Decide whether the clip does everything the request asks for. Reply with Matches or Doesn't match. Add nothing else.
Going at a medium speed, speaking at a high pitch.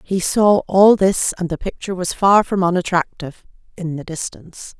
Doesn't match